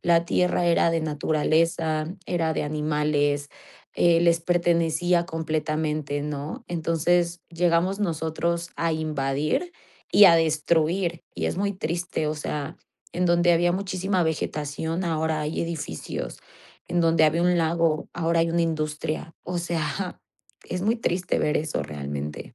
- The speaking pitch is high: No, medium, 165 Hz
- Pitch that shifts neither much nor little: No, narrow, 2.0 semitones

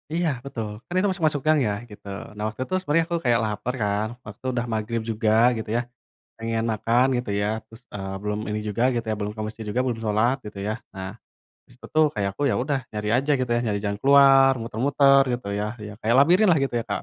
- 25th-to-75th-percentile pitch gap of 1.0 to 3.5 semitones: No, average, 4.5 semitones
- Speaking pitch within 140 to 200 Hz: No, low, 115 Hz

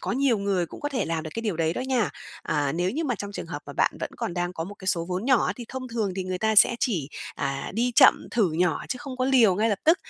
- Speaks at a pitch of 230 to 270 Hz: No, high, 205 Hz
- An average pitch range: No, wide, 5.9 semitones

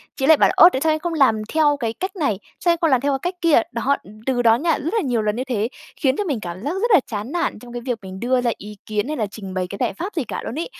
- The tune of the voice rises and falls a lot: Yes, wide, 6.2 semitones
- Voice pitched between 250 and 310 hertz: Yes, very high, 260 Hz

